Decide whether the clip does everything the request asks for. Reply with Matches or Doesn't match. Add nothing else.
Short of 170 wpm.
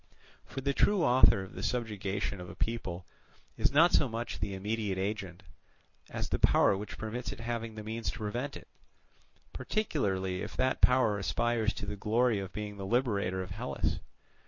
Doesn't match